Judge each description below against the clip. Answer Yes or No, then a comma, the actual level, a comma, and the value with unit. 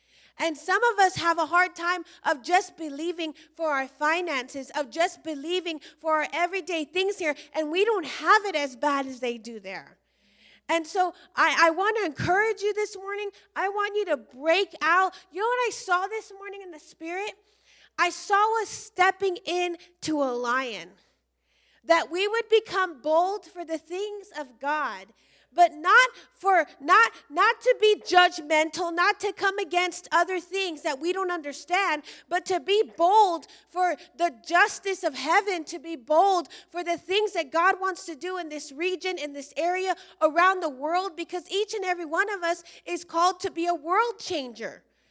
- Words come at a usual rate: Yes, average, 180 wpm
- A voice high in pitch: Yes, very high, 350 Hz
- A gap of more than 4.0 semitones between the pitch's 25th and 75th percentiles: No, average, 3.4 semitones